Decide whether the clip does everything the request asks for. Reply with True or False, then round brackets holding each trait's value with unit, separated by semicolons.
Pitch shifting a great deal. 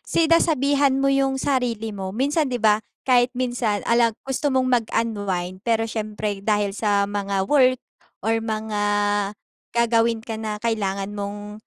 False (3.7 semitones)